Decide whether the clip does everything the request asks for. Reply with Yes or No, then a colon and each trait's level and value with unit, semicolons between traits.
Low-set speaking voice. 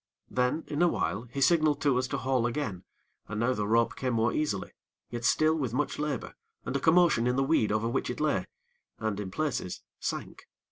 Yes: low, 125 Hz